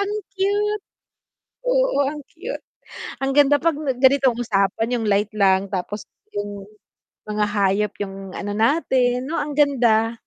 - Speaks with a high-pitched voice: Yes, high, 245 Hz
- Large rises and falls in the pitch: Yes, wide, 6.0 semitones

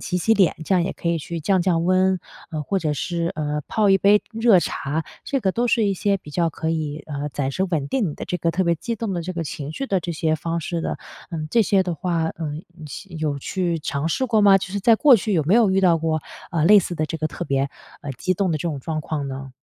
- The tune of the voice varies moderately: Yes, average, 3.8 semitones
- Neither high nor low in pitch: Yes, medium, 170 Hz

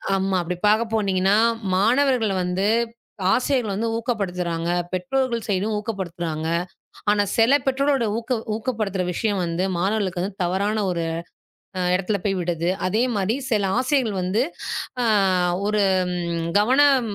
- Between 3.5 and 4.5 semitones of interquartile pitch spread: Yes, average, 4.0 semitones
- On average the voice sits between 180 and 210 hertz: Yes, high, 205 Hz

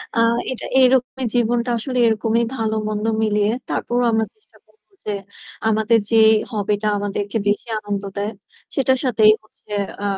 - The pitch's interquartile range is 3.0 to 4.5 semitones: No, narrow, 2.6 semitones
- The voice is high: Yes, high, 220 Hz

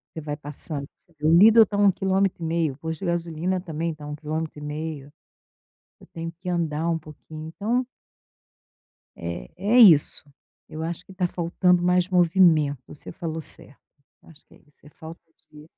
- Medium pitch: Yes, medium, 165 Hz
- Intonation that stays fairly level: No, average, 3.0 semitones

